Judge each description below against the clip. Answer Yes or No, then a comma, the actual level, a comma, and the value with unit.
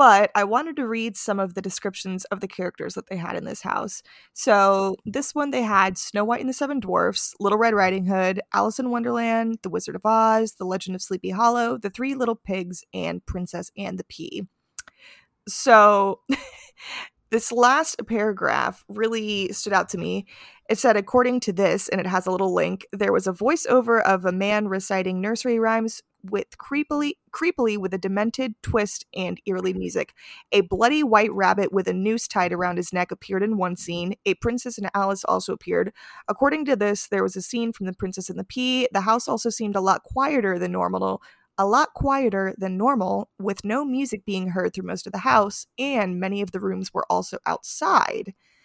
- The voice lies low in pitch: No, high, 205 Hz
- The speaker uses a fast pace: No, average, 195 wpm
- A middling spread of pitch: Yes, average, 3.7 semitones